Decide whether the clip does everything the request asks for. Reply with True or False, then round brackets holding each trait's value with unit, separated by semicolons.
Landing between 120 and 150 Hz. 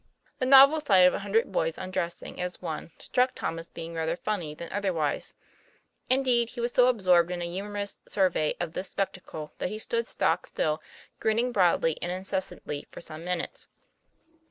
False (185 Hz)